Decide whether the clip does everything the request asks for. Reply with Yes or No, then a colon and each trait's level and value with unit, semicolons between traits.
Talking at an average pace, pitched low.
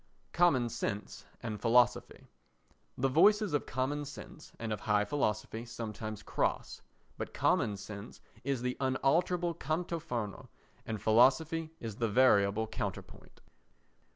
No: slow, 125 wpm; low, 125 Hz